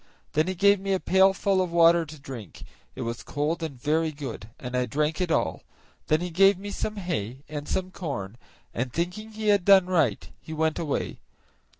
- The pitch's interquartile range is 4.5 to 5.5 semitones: Yes, average, 4.9 semitones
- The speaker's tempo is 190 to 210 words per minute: Yes, average, 200 wpm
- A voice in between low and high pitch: Yes, medium, 160 Hz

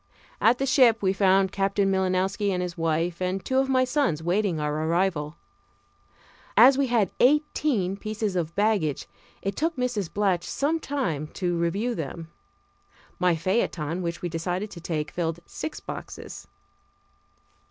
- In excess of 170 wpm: No, average, 150 wpm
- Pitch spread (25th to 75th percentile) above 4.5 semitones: Yes, average, 5.2 semitones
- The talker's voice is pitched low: No, high, 190 Hz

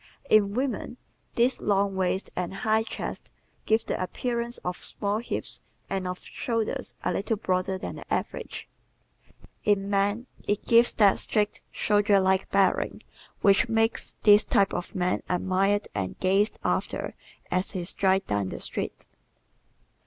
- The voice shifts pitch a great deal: No, narrow, 2.6 semitones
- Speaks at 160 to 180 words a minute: No, average, 145 wpm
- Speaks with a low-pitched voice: No, high, 200 Hz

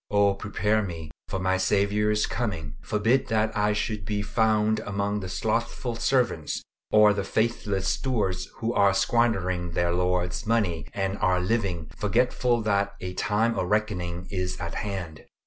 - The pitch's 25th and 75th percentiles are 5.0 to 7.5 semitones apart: No, average, 2.9 semitones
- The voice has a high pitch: No, low, 100 Hz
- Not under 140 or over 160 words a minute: Yes, average, 150 wpm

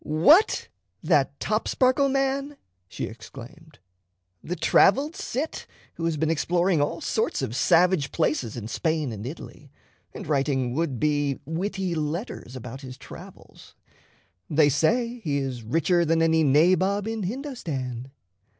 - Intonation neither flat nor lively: No, wide, 6.0 semitones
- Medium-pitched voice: Yes, medium, 160 Hz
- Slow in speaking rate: Yes, slow, 130 wpm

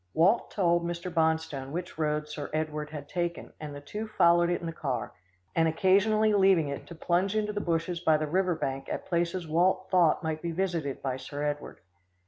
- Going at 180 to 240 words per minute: Yes, average, 200 wpm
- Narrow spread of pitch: No, average, 3.2 semitones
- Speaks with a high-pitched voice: No, medium, 170 Hz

